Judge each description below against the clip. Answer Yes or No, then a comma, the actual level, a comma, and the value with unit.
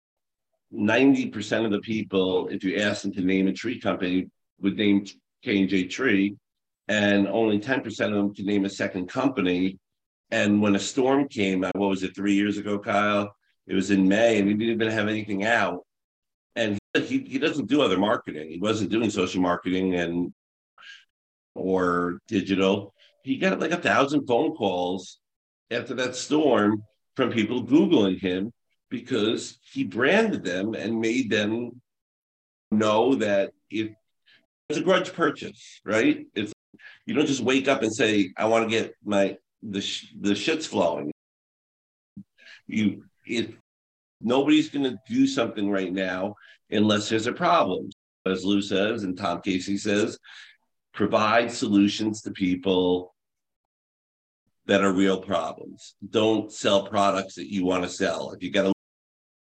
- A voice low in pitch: Yes, low, 100 Hz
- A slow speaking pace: No, average, 155 wpm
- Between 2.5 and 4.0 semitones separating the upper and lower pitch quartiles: Yes, average, 2.9 semitones